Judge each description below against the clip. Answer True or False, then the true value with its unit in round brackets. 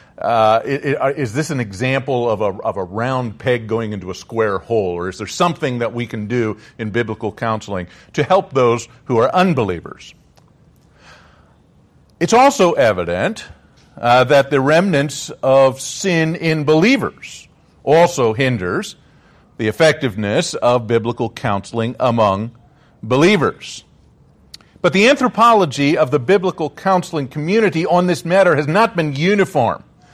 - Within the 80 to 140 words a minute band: True (135 wpm)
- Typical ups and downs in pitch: False (5.8 semitones)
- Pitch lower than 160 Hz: True (135 Hz)